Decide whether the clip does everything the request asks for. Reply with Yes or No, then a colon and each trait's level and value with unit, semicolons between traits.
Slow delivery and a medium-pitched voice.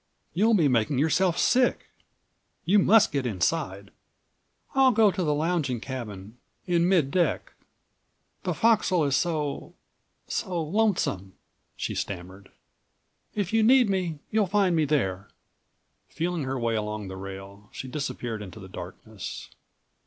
Yes: slow, 130 wpm; medium, 150 Hz